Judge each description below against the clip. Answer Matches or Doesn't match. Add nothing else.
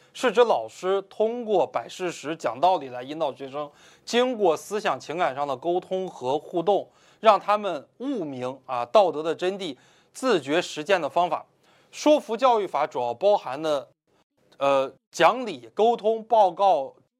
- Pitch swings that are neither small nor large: Doesn't match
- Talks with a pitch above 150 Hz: Matches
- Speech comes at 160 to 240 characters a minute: Matches